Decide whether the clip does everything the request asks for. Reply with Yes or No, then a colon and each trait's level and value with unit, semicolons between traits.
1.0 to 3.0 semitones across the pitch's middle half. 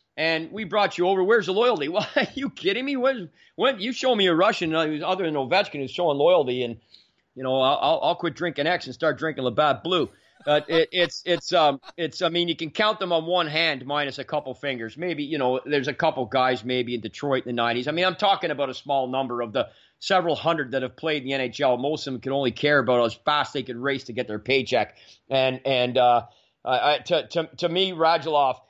No: average, 5.0 semitones